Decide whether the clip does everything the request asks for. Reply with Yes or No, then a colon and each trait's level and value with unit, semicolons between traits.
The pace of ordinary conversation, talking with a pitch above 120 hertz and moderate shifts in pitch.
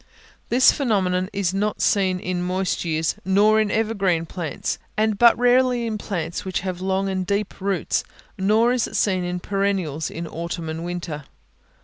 Yes: average, 165 wpm; high, 190 Hz; average, 3.1 semitones